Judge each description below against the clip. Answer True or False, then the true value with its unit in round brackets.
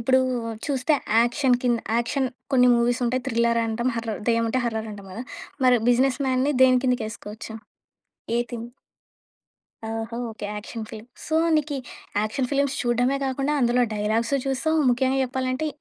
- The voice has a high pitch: True (245 Hz)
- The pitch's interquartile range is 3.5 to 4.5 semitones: False (2.4 semitones)